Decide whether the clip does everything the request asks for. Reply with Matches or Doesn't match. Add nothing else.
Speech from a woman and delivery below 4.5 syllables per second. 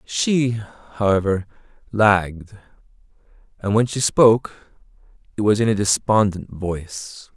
Doesn't match